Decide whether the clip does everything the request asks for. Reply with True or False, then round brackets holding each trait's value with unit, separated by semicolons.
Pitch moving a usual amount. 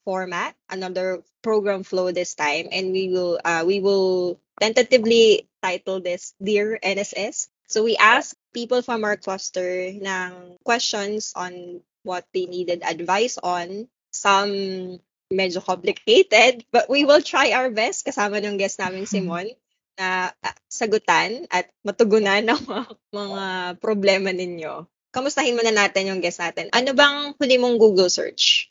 True (4.1 semitones)